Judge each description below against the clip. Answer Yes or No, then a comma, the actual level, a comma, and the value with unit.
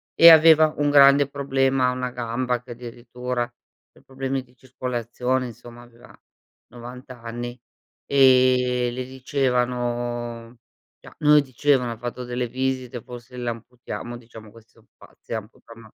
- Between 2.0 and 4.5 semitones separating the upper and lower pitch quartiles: No, narrow, 1.6 semitones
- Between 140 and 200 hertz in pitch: No, low, 125 Hz